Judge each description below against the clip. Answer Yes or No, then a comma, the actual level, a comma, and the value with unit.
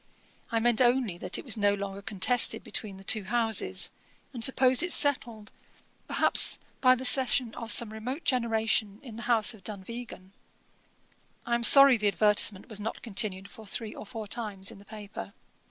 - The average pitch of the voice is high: Yes, high, 220 Hz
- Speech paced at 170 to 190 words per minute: Yes, average, 175 wpm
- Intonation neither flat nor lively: Yes, average, 3.0 semitones